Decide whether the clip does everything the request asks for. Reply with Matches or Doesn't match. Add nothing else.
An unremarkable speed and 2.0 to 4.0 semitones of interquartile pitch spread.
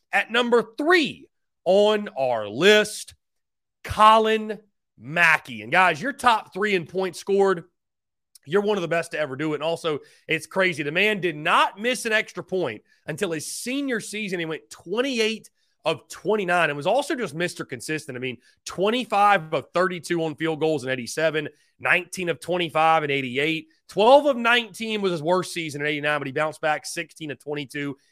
Doesn't match